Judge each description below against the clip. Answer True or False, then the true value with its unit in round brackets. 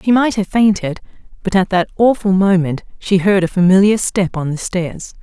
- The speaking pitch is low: False (190 Hz)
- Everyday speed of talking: True (195 wpm)